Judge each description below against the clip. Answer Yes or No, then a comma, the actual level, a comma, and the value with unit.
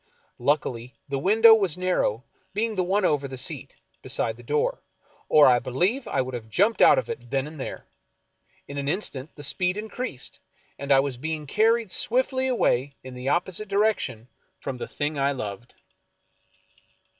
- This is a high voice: No, medium, 145 Hz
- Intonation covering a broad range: Yes, wide, 7.5 semitones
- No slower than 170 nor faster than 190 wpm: Yes, average, 175 wpm